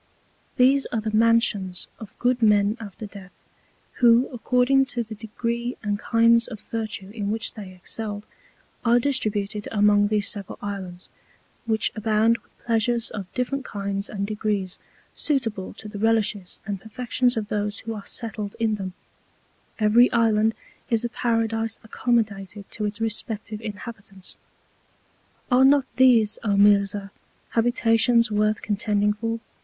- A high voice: Yes, high, 220 Hz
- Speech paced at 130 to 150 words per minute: Yes, average, 140 wpm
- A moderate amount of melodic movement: No, narrow, 2.2 semitones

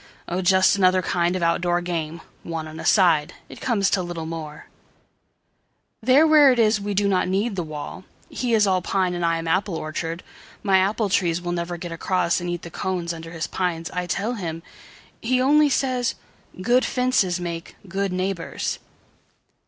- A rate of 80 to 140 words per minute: No, average, 170 wpm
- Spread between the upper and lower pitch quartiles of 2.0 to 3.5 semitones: Yes, average, 3.1 semitones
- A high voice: No, medium, 180 Hz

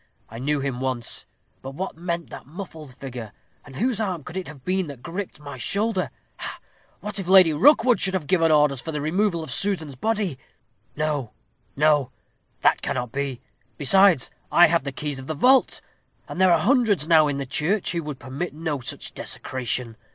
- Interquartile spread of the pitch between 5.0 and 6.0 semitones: Yes, wide, 5.5 semitones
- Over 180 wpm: Yes, average, 190 wpm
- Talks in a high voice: No, medium, 155 Hz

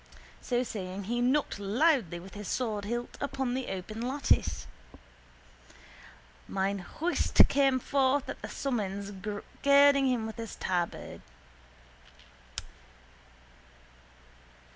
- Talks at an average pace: No, slow, 100 wpm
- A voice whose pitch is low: No, high, 240 Hz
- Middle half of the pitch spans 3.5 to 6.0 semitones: Yes, average, 5.2 semitones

